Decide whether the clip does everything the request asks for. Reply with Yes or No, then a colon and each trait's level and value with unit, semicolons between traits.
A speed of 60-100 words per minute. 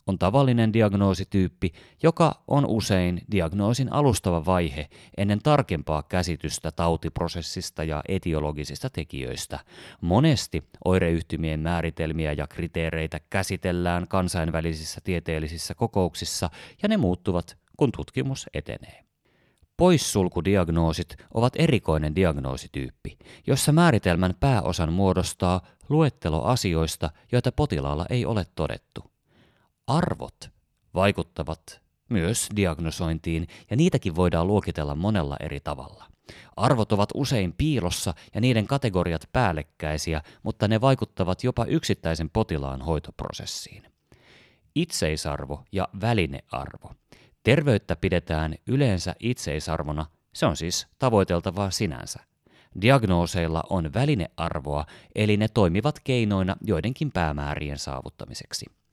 Yes: slow, 95 wpm